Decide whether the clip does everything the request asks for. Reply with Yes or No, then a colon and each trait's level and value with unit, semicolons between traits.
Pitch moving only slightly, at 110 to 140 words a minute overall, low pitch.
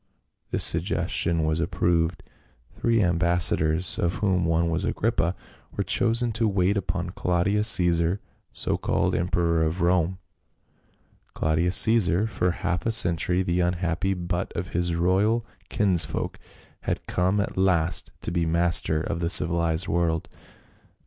Yes: narrow, 2.0 semitones; slow, 135 wpm; very low, 90 Hz